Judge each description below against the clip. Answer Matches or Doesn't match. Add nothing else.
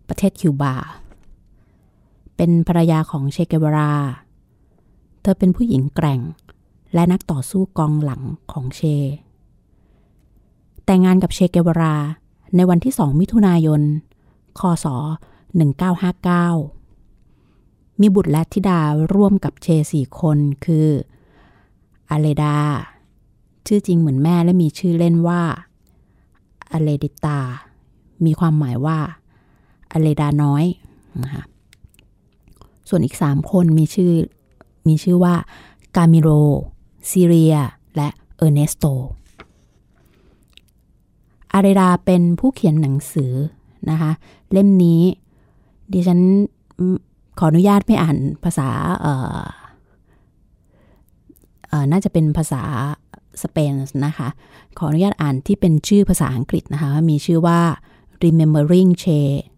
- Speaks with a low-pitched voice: Doesn't match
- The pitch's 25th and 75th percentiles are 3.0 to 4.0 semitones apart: Matches